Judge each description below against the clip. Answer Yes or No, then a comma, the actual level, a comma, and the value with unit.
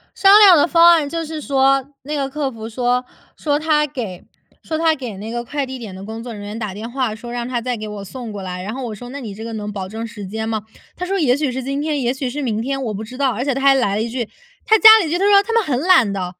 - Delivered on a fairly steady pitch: No, average, 4.8 semitones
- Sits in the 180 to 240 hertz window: No, very high, 250 Hz